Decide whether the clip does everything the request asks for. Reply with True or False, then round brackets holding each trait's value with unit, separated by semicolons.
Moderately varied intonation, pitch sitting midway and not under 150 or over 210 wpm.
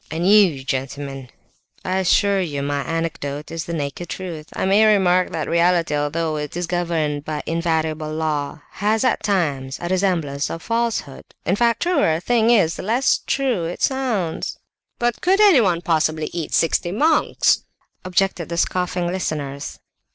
True (4.4 semitones; 170 Hz; 160 wpm)